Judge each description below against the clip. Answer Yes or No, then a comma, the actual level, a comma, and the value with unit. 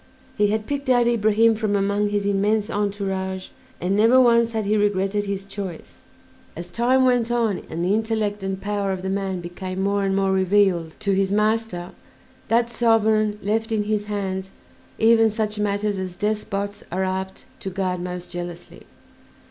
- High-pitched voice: Yes, high, 205 Hz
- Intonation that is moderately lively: No, narrow, 2.3 semitones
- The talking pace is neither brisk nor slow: Yes, average, 170 wpm